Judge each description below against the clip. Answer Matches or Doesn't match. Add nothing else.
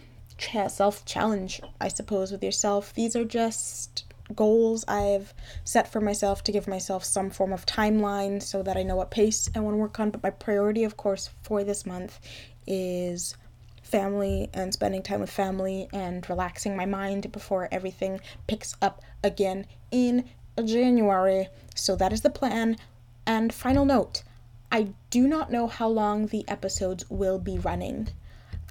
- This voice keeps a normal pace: Matches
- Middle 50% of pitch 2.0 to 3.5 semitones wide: Matches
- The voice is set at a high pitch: Matches